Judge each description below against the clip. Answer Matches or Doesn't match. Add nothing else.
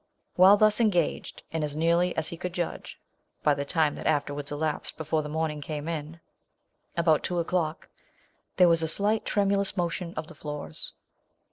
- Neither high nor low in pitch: Matches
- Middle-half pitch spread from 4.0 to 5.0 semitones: Doesn't match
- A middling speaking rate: Matches